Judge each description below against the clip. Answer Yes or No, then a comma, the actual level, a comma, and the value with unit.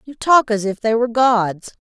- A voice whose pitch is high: Yes, high, 230 Hz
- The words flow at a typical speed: No, fast, 225 wpm